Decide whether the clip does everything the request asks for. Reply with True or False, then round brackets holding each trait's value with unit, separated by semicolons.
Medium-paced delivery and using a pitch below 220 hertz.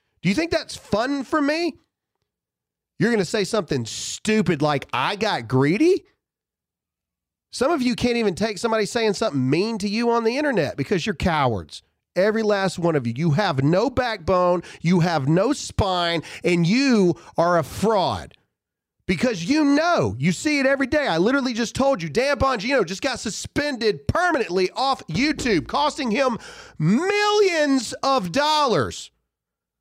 False (160 wpm; 225 Hz)